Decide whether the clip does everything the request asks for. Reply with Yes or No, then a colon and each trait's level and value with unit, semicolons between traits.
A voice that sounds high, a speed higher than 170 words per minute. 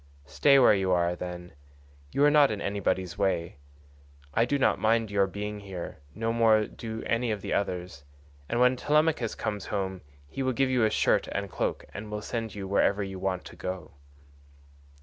No: low, 105 Hz; average, 190 wpm